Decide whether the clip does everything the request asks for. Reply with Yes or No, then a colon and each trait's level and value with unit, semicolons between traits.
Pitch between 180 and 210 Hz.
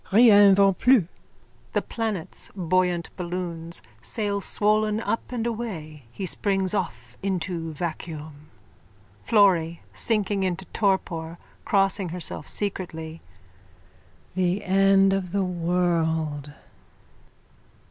Yes: medium, 185 Hz